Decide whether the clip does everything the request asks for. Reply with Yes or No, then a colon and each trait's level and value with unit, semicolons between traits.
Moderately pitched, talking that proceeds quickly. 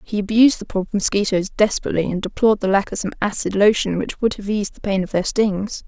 No: high, 200 Hz; fast, 235 wpm